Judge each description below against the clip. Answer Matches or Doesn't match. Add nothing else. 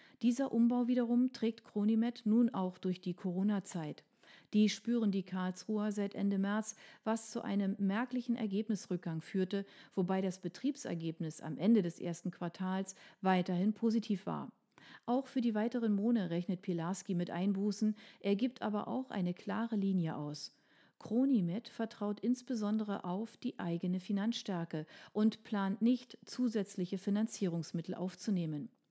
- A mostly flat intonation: Doesn't match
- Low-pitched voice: Doesn't match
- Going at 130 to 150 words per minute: Matches